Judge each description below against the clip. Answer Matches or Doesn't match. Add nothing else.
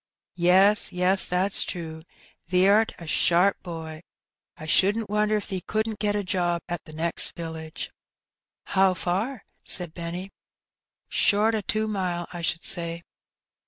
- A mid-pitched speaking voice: Matches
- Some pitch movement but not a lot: Matches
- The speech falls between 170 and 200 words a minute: Doesn't match